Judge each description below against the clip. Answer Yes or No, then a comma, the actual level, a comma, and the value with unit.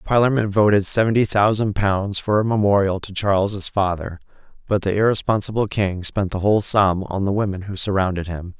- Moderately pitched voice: No, low, 100 Hz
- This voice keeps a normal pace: Yes, average, 175 wpm